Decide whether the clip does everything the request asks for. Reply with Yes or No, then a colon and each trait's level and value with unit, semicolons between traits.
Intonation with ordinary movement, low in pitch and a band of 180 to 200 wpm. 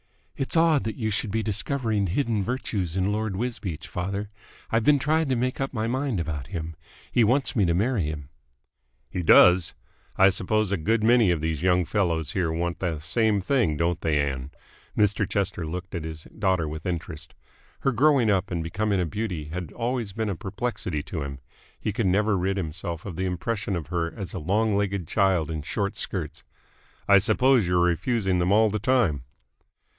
Yes: average, 4.7 semitones; very low, 95 Hz; average, 190 wpm